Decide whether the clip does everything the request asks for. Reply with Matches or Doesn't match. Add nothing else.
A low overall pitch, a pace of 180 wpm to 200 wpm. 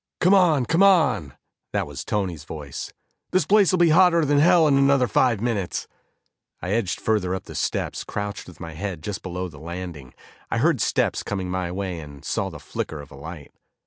Matches